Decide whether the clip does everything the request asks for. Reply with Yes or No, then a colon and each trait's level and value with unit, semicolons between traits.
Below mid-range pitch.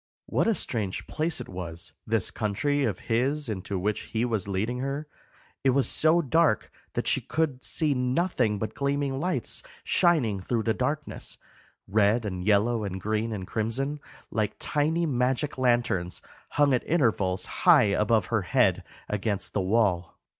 Yes: low, 115 Hz